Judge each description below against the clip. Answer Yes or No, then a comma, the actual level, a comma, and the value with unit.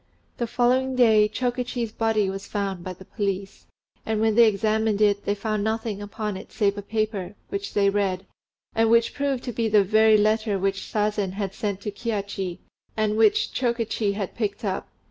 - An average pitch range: No, narrow, 2.0 semitones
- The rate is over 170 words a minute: Yes, average, 185 wpm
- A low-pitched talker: No, high, 210 Hz